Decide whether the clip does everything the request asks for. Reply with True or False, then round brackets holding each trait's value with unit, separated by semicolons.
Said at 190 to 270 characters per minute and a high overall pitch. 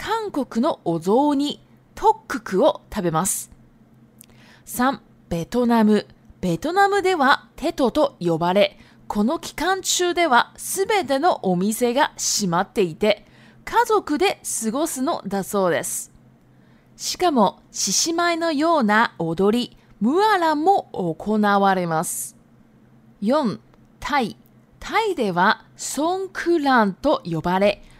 True (210 characters per minute; 240 Hz)